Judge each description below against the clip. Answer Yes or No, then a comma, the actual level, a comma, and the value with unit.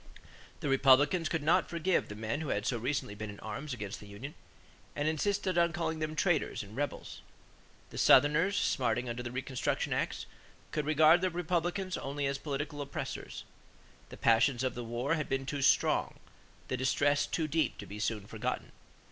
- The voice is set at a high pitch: No, medium, 145 Hz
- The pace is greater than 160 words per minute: Yes, average, 180 wpm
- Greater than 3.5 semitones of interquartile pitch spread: Yes, average, 4.7 semitones